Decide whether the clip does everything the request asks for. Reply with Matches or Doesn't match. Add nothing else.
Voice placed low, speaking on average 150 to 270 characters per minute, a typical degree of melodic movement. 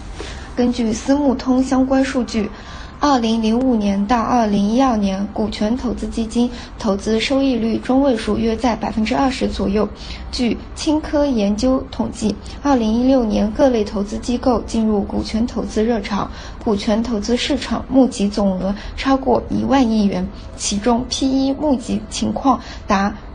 Doesn't match